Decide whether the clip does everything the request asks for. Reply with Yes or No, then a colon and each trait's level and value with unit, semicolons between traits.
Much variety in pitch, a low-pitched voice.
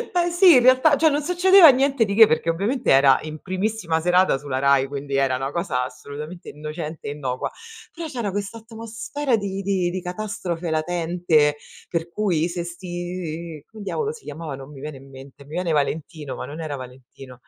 No: wide, 6.6 semitones; medium, 175 Hz